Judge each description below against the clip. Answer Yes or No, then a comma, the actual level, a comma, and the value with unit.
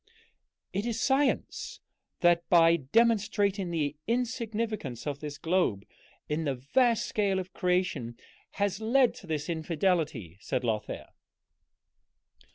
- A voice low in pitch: No, medium, 180 Hz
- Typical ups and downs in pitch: No, wide, 6.7 semitones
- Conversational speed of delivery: No, slow, 115 wpm